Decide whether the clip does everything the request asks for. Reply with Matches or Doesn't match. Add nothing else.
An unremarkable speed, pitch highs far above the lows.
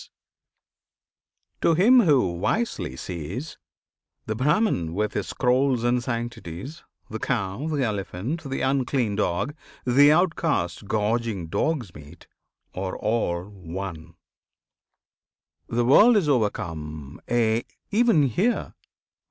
Doesn't match